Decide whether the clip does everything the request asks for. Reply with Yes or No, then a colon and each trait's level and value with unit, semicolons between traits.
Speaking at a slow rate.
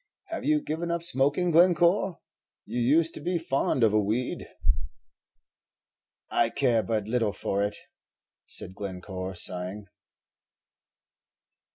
Yes: slow, 115 wpm